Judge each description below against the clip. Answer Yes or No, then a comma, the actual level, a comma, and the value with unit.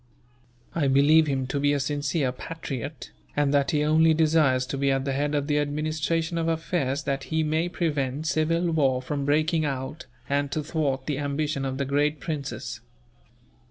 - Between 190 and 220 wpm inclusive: No, average, 180 wpm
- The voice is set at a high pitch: No, medium, 145 Hz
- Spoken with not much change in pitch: Yes, narrow, 2.3 semitones